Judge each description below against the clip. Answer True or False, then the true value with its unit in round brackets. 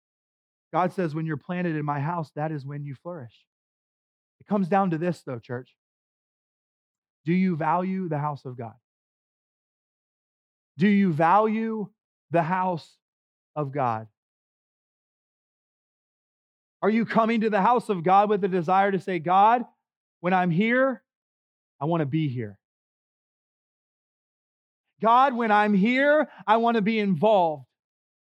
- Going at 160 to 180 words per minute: False (140 wpm)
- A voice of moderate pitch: True (180 Hz)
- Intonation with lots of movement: True (5.8 semitones)